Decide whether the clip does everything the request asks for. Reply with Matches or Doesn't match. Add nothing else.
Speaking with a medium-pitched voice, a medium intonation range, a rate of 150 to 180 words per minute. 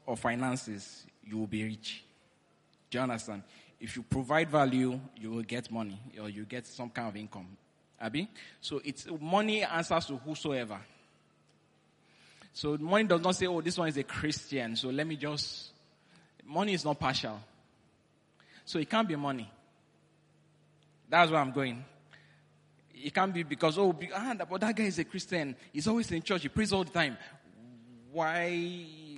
Doesn't match